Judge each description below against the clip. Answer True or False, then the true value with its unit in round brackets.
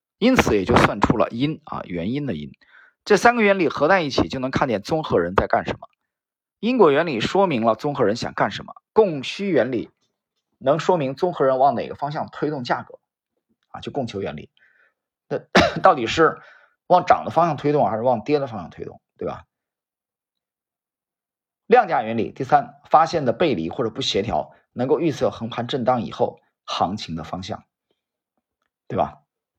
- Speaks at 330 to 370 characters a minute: False (260 characters per minute)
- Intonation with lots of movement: True (8.1 semitones)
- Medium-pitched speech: True (145 Hz)